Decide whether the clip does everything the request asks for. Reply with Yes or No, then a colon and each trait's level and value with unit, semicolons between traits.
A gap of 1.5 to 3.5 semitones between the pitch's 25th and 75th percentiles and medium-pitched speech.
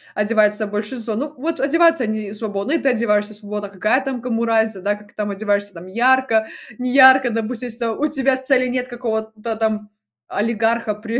No: average, 3.2 semitones; high, 225 Hz